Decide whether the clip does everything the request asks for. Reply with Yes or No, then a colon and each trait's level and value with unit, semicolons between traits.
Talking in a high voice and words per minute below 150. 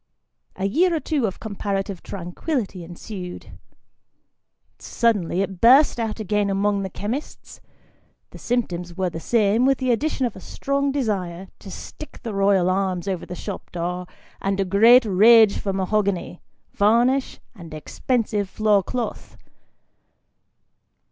Yes: high, 200 Hz; slow, 135 wpm